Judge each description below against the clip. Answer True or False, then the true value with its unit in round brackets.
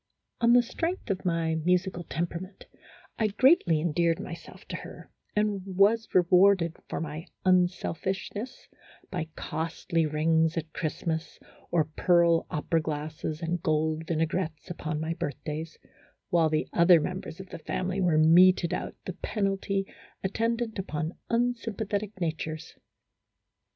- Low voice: False (170 Hz)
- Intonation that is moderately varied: True (3.3 semitones)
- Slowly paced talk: True (130 wpm)